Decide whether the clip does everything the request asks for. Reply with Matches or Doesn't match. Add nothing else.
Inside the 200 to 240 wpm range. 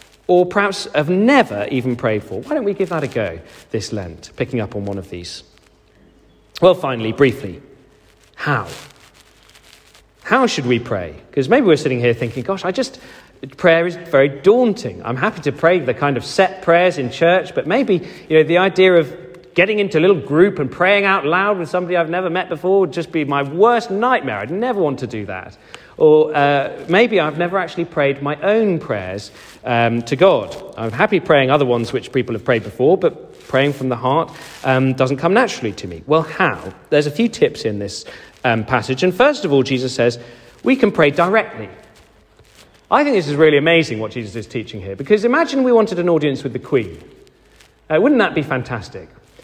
Matches